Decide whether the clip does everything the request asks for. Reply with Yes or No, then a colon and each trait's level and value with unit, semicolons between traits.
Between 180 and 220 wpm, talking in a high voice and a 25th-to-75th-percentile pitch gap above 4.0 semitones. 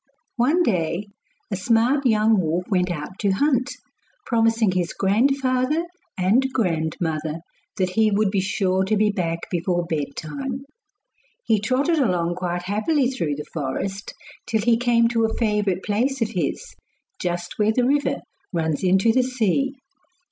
No: average, 150 wpm; high, 210 Hz; wide, 5.5 semitones